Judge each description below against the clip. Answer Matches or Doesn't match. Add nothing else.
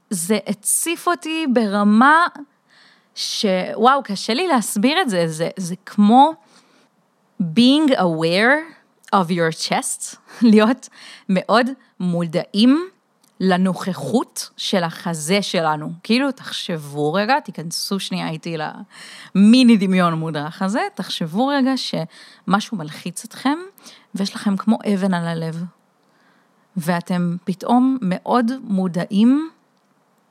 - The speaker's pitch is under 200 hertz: Doesn't match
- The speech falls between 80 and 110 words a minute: Matches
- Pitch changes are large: Matches